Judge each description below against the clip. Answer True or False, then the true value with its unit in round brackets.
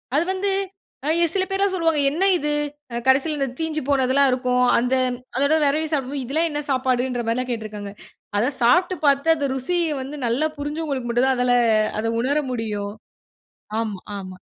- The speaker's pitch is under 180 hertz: False (270 Hz)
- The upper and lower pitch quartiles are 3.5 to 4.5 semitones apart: True (4.0 semitones)